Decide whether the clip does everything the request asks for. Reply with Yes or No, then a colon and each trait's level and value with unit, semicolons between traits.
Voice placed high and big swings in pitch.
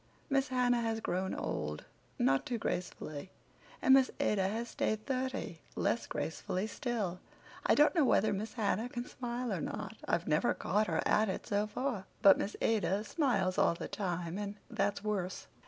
No: high, 215 Hz; average, 4.2 semitones